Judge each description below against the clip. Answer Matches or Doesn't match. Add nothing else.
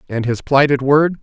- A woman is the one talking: Doesn't match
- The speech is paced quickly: Doesn't match